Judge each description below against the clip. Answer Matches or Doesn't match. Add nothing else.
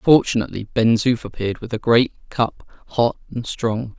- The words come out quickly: Doesn't match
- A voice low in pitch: Matches